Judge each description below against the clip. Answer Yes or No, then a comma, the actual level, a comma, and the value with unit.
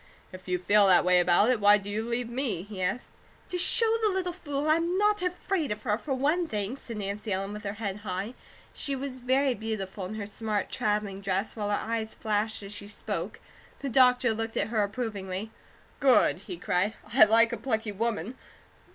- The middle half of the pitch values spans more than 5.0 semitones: No, average, 4.2 semitones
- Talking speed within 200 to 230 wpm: Yes, fast, 205 wpm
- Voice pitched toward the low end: No, high, 220 Hz